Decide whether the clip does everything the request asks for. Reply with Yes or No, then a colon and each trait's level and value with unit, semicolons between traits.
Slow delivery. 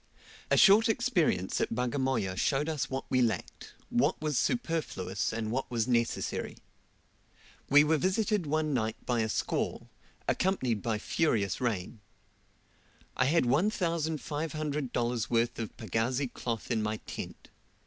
Yes: slow, 130 wpm